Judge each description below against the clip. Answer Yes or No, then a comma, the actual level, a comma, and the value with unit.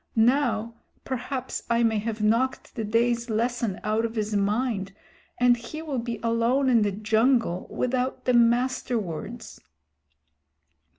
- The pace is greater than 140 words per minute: No, slow, 135 wpm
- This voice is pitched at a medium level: No, high, 230 Hz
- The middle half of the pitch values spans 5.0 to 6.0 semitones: No, narrow, 2.4 semitones